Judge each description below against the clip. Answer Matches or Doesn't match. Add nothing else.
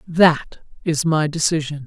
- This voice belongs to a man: Doesn't match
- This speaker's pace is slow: Matches